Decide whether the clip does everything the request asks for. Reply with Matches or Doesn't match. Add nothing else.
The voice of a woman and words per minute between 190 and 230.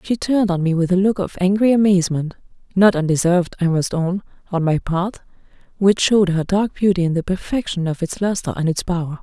Matches